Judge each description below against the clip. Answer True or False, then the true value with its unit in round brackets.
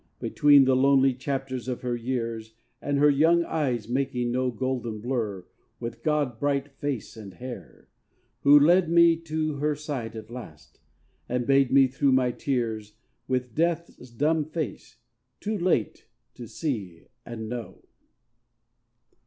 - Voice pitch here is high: False (130 Hz)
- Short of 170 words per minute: True (140 wpm)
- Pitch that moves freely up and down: False (3.7 semitones)